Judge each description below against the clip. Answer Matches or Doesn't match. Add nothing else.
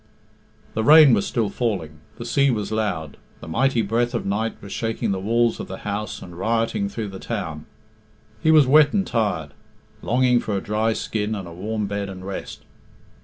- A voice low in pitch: Matches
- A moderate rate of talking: Matches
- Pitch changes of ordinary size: Matches